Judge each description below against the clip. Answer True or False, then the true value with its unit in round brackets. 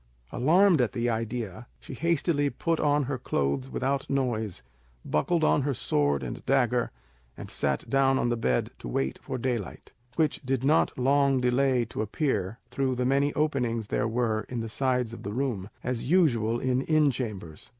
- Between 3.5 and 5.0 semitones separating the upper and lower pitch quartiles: True (3.8 semitones)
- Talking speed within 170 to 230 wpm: True (175 wpm)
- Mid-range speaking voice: False (125 Hz)